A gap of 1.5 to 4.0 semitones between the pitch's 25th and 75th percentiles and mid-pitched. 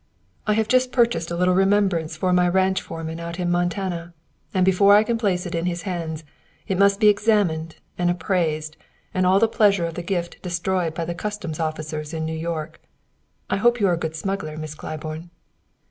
Yes: average, 3.2 semitones; medium, 175 Hz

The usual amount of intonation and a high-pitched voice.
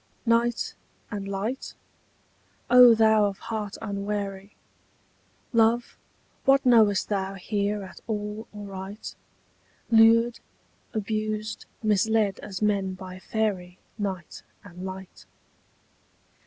No: narrow, 2.2 semitones; high, 210 Hz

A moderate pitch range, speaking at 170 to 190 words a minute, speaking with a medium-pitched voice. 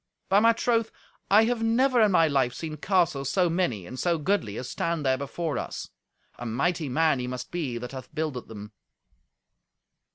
No: wide, 6.9 semitones; average, 185 wpm; medium, 160 Hz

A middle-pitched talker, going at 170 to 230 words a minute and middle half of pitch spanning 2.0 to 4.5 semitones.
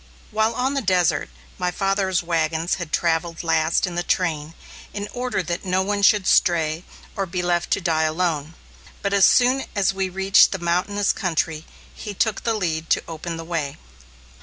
Yes: medium, 180 Hz; average, 180 wpm; average, 3.3 semitones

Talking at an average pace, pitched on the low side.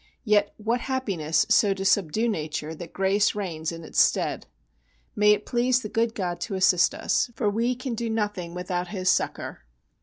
No: average, 180 wpm; high, 205 Hz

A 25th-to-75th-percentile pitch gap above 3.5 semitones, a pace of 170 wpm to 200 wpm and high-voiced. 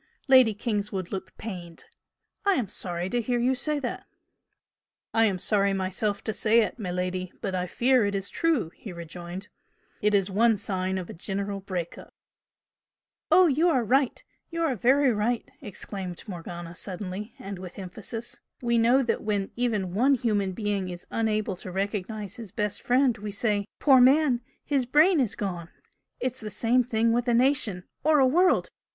Yes: average, 4.6 semitones; average, 175 wpm; high, 210 Hz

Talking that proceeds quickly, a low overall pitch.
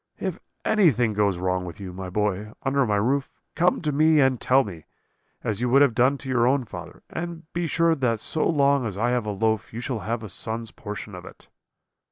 Yes: fast, 225 wpm; low, 120 Hz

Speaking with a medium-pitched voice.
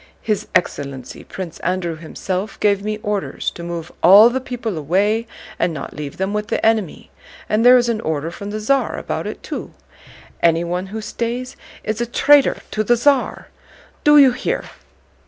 No: high, 210 Hz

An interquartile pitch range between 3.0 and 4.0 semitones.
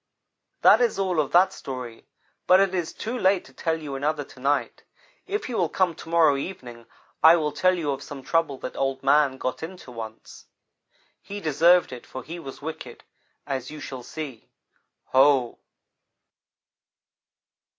No: average, 4.6 semitones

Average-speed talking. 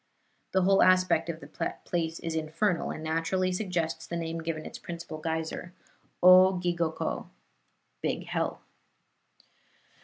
No: slow, 125 wpm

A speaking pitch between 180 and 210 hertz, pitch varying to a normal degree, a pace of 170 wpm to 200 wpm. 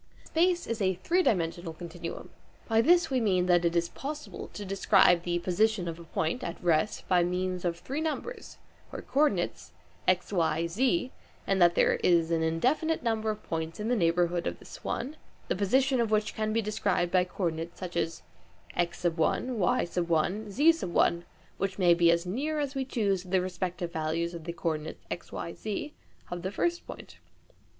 Yes: medium, 185 Hz; average, 4.7 semitones; average, 185 wpm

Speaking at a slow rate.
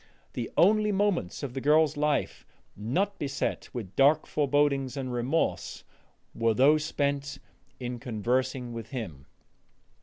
Yes: slow, 125 wpm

